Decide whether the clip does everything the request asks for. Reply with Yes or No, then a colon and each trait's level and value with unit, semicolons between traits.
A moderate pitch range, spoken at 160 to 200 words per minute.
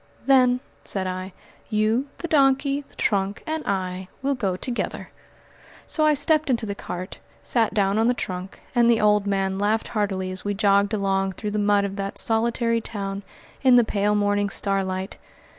Yes: average, 3.4 semitones; average, 175 wpm